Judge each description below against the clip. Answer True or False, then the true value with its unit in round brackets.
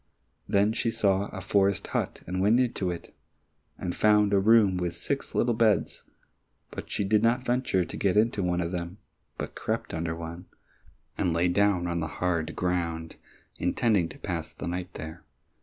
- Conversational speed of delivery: True (175 wpm)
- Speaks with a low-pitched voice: True (95 Hz)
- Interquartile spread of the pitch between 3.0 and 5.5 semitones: True (3.4 semitones)